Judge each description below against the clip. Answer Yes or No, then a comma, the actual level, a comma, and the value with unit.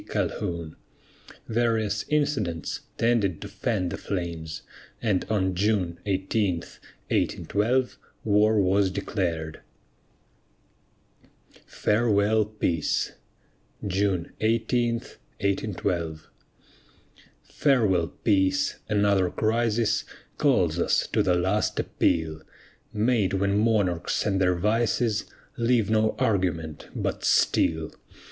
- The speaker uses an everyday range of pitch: Yes, average, 3.6 semitones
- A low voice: Yes, low, 100 Hz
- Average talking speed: No, slow, 90 wpm